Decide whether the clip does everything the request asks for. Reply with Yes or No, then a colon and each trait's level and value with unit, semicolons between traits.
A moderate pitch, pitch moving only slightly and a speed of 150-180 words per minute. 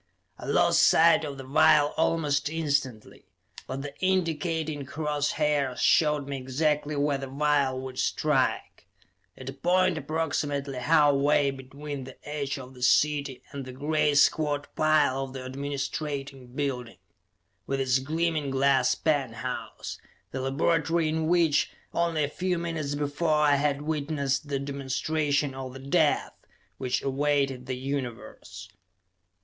No: medium, 145 Hz; narrow, 2.2 semitones; average, 140 wpm